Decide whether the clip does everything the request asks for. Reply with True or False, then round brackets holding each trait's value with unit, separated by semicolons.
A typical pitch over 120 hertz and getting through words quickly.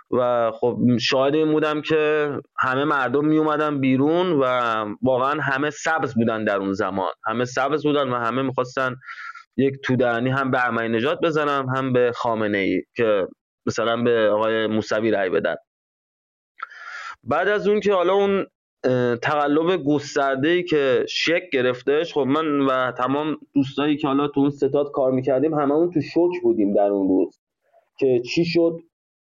False (140 Hz; 160 wpm)